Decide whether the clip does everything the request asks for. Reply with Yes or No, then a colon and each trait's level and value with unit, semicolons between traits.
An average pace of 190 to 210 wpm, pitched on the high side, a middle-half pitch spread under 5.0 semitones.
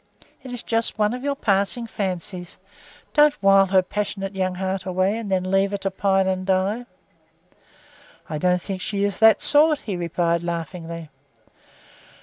No: average, 160 wpm; high, 195 Hz; narrow, 2.5 semitones